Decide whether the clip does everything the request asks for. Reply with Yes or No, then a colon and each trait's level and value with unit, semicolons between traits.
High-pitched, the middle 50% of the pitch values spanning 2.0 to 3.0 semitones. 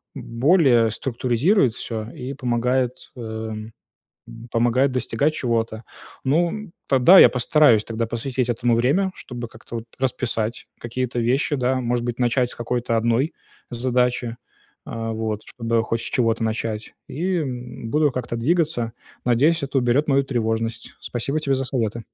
No: low, 120 Hz; narrow, 2.6 semitones